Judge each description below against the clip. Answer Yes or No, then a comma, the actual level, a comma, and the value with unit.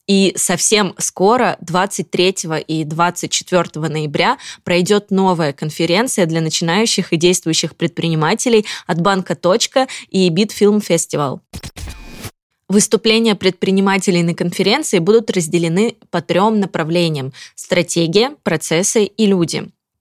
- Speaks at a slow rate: Yes, slow, 100 wpm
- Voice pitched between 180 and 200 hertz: Yes, medium, 185 Hz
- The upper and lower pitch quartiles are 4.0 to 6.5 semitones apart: No, average, 3.3 semitones